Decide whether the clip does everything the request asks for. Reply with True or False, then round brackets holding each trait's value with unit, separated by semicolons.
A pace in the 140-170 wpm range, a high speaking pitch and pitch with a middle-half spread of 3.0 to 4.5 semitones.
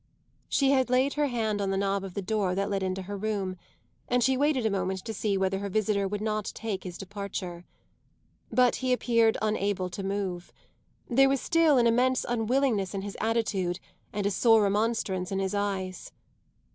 False (190 wpm; 205 Hz; 3.4 semitones)